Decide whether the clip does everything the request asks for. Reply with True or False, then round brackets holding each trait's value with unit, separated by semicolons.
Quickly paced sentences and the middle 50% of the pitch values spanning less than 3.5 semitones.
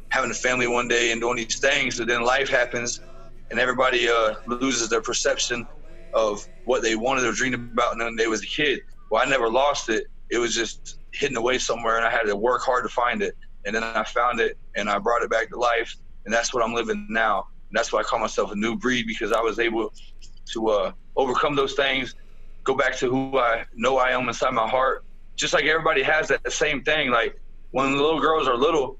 True (235 wpm; 2.4 semitones)